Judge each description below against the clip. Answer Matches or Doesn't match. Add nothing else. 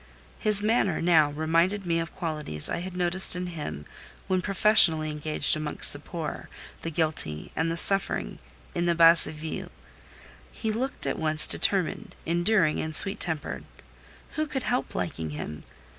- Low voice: Doesn't match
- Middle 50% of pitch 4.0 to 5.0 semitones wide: Doesn't match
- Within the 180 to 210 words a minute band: Doesn't match